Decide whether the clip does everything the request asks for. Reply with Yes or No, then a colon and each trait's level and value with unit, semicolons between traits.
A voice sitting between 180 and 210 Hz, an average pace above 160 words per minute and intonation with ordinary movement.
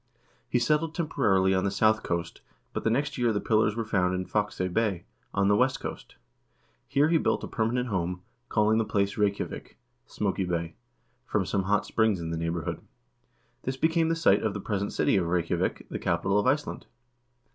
No: low, 105 Hz; average, 190 wpm; average, 4.5 semitones